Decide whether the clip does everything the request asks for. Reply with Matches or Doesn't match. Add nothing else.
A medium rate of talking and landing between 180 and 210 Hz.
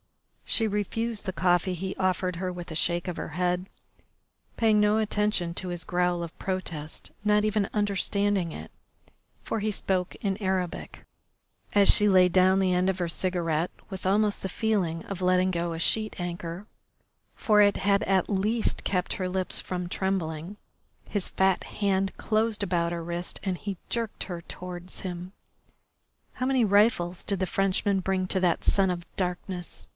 Matches